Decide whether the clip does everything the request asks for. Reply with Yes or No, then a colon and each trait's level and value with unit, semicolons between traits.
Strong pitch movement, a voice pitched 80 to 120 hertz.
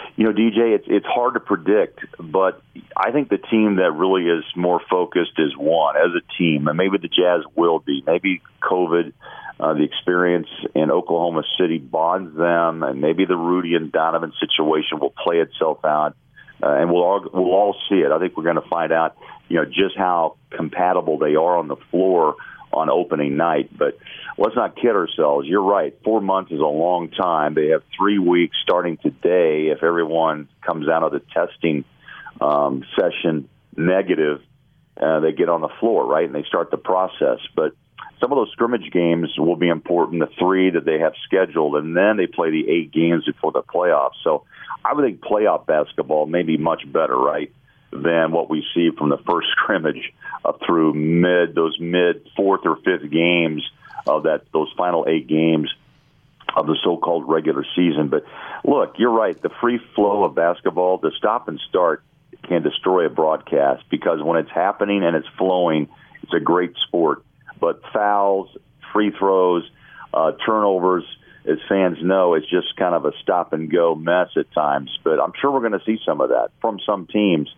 No: average, 2.8 semitones; very low, 85 Hz